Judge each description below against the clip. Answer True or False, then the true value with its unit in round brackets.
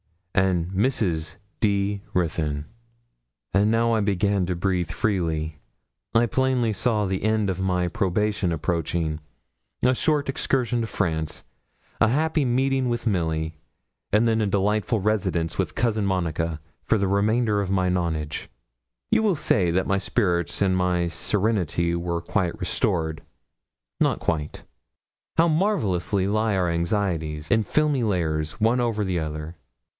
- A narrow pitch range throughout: False (4.6 semitones)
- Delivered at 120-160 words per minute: True (140 wpm)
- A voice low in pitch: True (95 Hz)